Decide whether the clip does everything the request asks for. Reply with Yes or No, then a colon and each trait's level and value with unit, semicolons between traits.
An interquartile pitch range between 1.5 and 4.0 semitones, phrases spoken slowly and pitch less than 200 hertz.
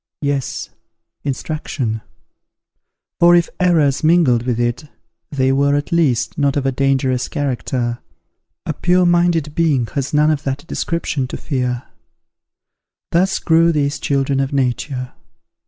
Yes: average, 3.6 semitones; slow, 130 wpm; medium, 140 Hz